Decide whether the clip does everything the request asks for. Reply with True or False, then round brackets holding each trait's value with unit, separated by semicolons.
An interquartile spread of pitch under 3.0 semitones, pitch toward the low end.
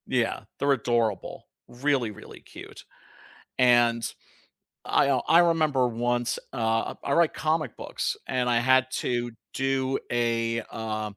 True (2.5 semitones; 120 Hz)